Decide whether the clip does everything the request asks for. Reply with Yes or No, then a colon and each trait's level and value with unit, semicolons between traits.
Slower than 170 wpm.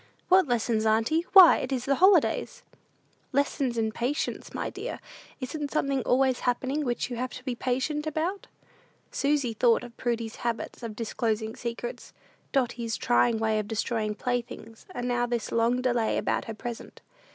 Yes: average, 160 wpm